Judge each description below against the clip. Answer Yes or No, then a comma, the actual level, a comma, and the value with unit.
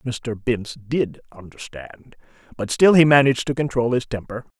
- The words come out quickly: No, average, 155 wpm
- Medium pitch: No, low, 125 Hz